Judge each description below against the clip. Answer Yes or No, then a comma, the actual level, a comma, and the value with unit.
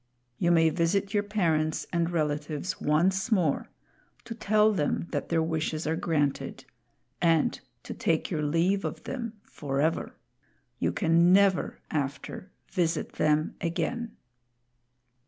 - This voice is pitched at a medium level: Yes, medium, 165 Hz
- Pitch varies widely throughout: No, average, 4.1 semitones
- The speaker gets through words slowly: Yes, slow, 125 wpm